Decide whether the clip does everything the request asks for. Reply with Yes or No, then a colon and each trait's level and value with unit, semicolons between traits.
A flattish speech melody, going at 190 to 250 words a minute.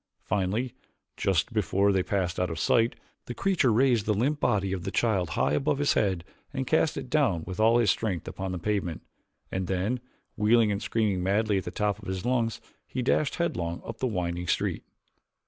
No: average, 4.4 semitones; average, 200 wpm